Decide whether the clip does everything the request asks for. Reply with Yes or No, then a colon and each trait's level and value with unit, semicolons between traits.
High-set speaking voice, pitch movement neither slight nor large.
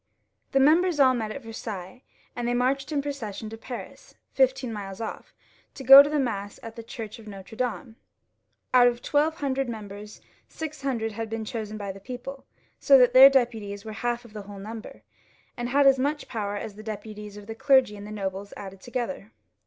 Yes: high, 230 Hz; average, 4.0 semitones